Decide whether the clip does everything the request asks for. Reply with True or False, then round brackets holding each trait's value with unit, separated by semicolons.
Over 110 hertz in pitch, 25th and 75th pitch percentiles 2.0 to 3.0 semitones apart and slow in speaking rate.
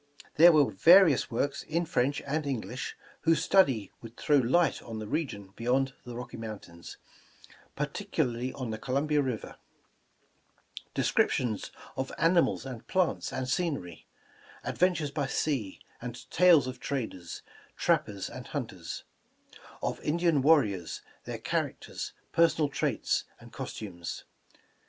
False (135 Hz; 5.1 semitones; 130 wpm)